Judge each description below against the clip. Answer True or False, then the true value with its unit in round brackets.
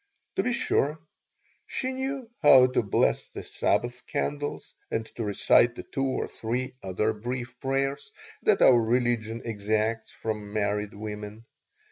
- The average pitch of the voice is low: True (120 Hz)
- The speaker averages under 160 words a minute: True (140 wpm)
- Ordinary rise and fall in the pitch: True (4.0 semitones)